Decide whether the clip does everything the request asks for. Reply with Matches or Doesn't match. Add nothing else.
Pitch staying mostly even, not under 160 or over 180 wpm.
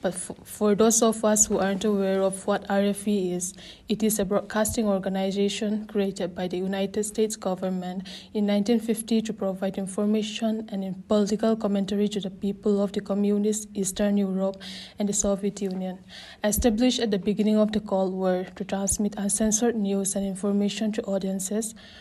Matches